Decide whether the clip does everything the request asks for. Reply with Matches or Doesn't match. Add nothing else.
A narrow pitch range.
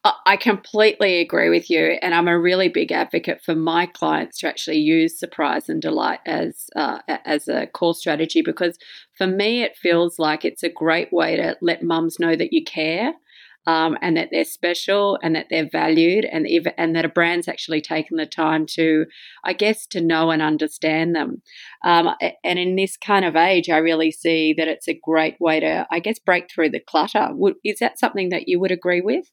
Doesn't match